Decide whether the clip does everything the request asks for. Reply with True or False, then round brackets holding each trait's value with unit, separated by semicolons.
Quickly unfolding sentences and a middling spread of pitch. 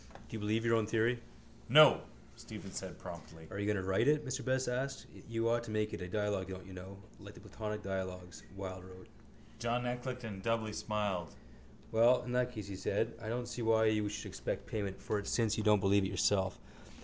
True (215 wpm; 3.2 semitones)